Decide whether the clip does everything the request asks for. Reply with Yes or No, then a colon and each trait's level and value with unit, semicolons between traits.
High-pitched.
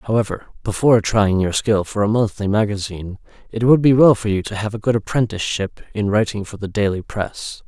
No: low, 105 Hz